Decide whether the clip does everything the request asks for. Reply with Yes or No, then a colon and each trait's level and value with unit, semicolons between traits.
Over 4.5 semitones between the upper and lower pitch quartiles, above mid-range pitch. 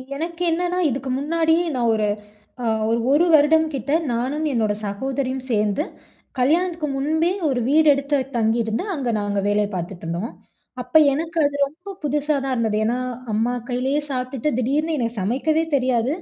Yes: average, 5.0 semitones; very high, 270 Hz